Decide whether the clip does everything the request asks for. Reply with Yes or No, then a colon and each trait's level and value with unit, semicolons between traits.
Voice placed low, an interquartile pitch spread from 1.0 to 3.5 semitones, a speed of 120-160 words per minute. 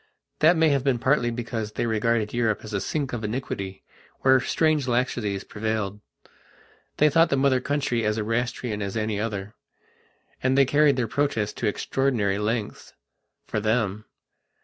No: low, 115 Hz; average, 3.9 semitones; average, 155 wpm